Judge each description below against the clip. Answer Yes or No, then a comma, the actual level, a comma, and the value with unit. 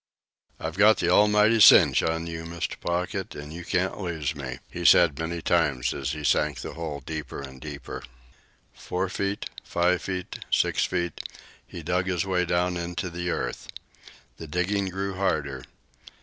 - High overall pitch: No, very low, 85 Hz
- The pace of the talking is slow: No, average, 165 wpm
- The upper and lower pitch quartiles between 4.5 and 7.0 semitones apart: No, average, 2.9 semitones